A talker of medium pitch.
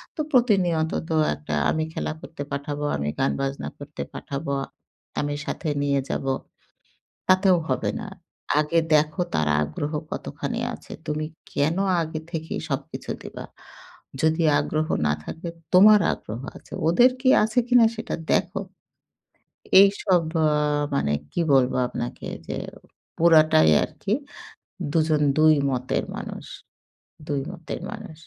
Yes: medium, 155 Hz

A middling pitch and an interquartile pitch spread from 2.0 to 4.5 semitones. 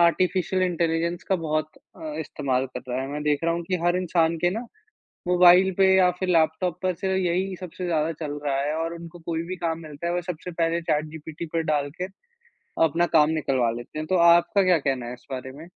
Yes: medium, 165 Hz; average, 2.8 semitones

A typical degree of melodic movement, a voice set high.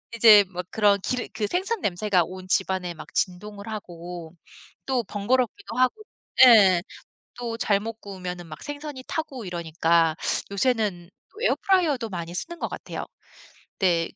No: wide, 5.8 semitones; high, 205 Hz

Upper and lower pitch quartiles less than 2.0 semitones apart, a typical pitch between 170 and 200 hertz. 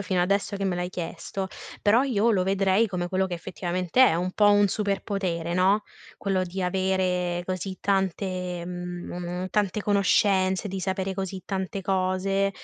Yes: narrow, 1.6 semitones; high, 190 Hz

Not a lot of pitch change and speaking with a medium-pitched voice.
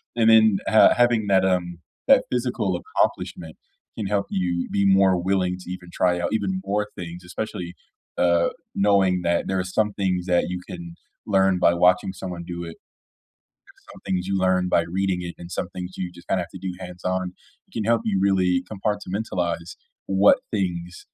No: narrow, 2.0 semitones; very low, 95 Hz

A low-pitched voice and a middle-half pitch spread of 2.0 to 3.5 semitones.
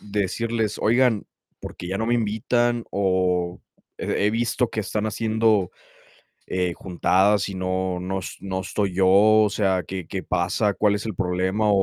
Yes: low, 100 Hz; average, 2.8 semitones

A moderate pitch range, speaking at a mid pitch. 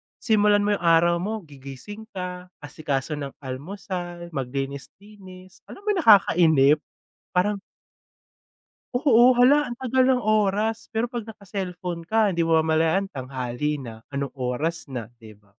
No: wide, 6.8 semitones; medium, 180 Hz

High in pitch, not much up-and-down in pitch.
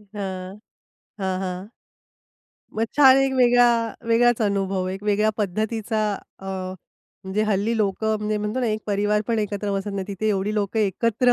Yes: high, 210 Hz; narrow, 2.3 semitones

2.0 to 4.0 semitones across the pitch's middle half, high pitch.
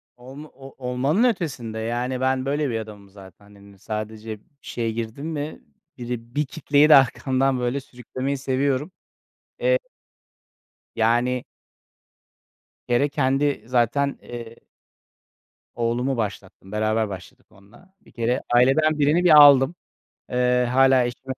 No: average, 3.5 semitones; low, 125 Hz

